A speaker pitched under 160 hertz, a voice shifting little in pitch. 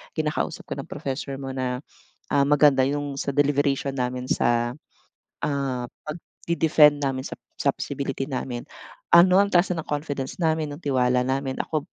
Yes: medium, 140 Hz; narrow, 2.1 semitones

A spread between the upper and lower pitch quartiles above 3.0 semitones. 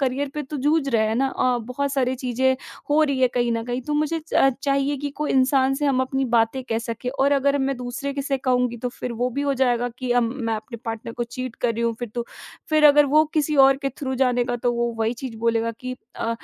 No: narrow, 2.6 semitones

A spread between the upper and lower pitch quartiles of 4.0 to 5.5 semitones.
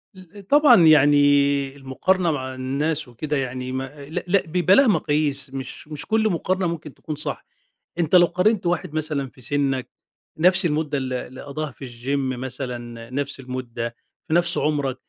Yes: average, 4.3 semitones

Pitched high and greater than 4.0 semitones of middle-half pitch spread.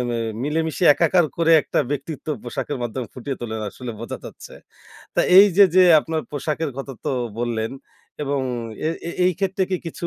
No: medium, 145 Hz; average, 4.9 semitones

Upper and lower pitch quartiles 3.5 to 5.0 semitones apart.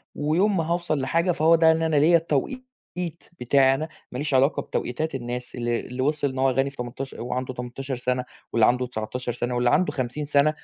Yes: average, 4.2 semitones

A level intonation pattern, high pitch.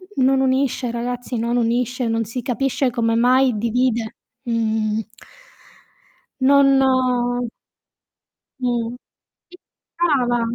Yes: narrow, 2.0 semitones; high, 245 Hz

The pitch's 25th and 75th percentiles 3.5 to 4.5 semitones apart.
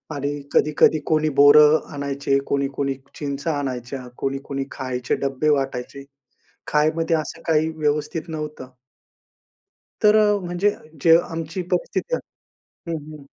No: average, 2.8 semitones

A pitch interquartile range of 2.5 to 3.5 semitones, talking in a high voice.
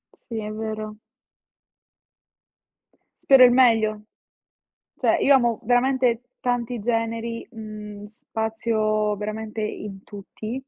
No: narrow, 2.0 semitones; high, 220 Hz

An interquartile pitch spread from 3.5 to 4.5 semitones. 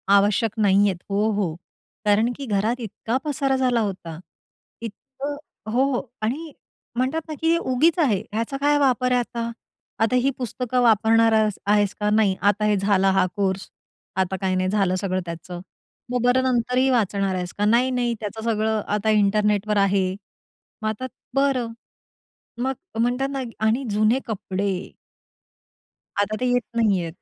Yes: average, 4.0 semitones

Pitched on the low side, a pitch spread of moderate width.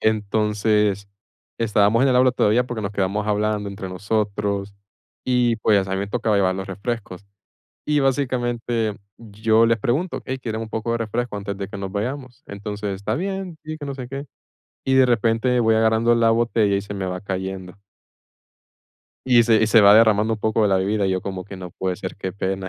Yes: low, 110 Hz; average, 3.0 semitones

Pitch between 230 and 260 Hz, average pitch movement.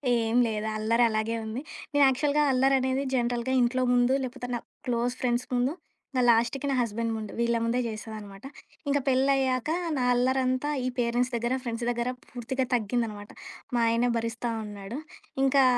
No: high, 245 Hz; narrow, 2.1 semitones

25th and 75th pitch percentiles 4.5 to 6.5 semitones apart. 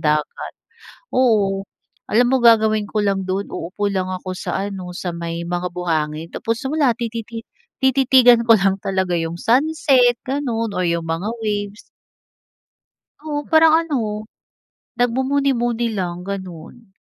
Yes: average, 4.9 semitones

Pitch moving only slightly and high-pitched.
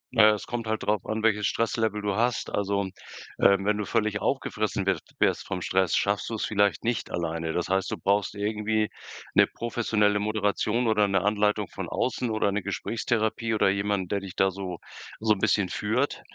No: narrow, 1.9 semitones; low, 105 Hz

